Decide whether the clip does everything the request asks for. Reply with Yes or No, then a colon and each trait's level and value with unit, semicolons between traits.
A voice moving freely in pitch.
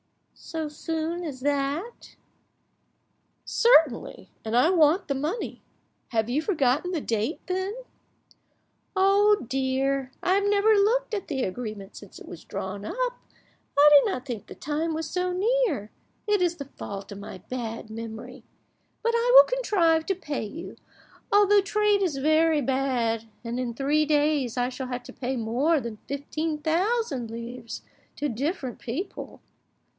Yes: wide, 6.9 semitones